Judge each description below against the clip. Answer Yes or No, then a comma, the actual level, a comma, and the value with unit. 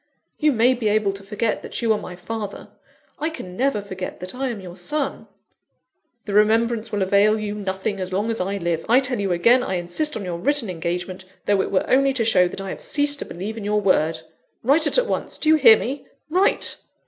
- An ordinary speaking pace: No, fast, 225 wpm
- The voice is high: Yes, high, 210 Hz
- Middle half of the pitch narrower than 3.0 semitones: No, average, 5.0 semitones